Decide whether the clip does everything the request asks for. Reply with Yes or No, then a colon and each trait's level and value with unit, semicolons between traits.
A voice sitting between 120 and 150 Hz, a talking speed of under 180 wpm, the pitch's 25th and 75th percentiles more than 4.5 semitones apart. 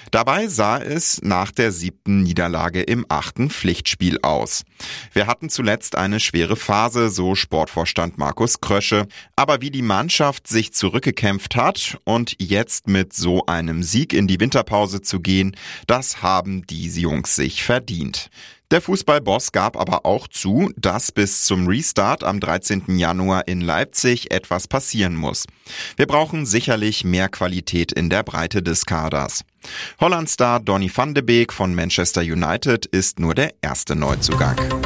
No: very low, 95 Hz; average, 150 wpm; average, 5.0 semitones